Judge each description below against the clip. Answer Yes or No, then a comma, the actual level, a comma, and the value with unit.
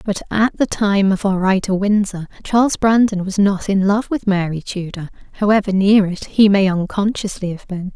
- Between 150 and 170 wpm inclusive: No, average, 195 wpm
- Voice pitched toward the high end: Yes, high, 200 Hz